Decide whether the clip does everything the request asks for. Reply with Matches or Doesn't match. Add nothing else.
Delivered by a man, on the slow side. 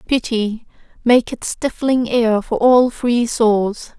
Doesn't match